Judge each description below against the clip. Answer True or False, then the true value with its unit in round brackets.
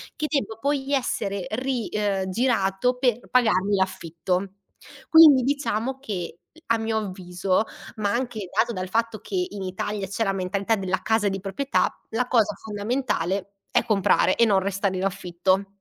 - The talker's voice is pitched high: True (205 Hz)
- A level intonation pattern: False (3.7 semitones)